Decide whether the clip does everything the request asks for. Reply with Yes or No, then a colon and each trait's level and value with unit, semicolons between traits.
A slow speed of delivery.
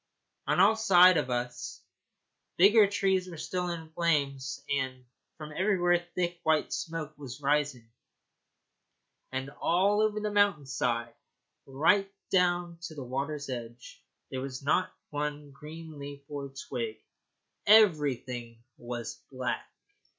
Yes: slow, 130 wpm